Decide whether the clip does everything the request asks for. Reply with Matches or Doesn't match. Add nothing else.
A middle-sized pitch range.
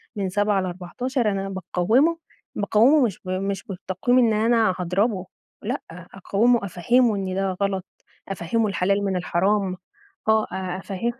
Matches